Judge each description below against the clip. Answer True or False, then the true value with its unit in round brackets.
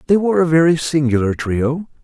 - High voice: False (150 Hz)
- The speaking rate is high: False (175 wpm)